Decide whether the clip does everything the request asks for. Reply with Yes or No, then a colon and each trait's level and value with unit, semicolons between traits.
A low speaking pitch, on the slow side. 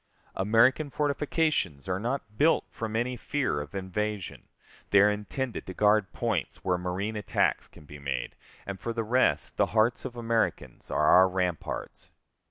No: low, 105 Hz; average, 160 wpm